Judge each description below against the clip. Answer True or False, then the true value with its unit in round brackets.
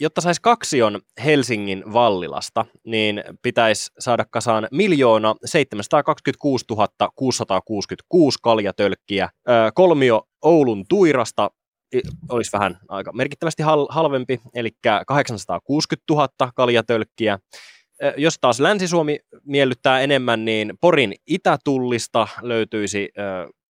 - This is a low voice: True (120 Hz)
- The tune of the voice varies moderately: True (4.7 semitones)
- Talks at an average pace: False (85 wpm)